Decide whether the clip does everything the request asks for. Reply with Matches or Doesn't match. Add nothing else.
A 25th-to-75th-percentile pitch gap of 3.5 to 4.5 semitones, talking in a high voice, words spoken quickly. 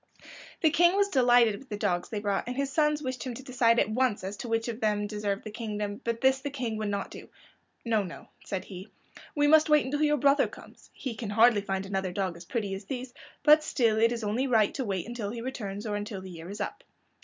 Matches